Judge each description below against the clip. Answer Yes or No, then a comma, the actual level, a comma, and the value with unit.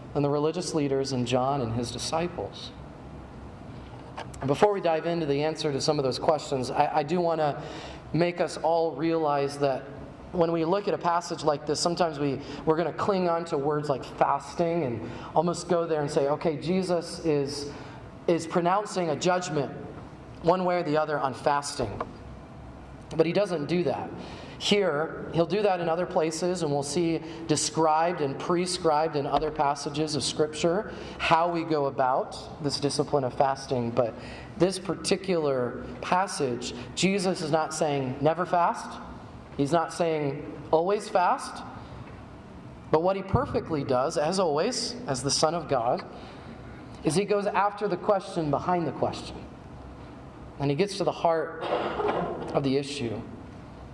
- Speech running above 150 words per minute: Yes, average, 160 wpm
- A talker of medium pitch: Yes, medium, 155 Hz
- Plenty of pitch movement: No, average, 3.3 semitones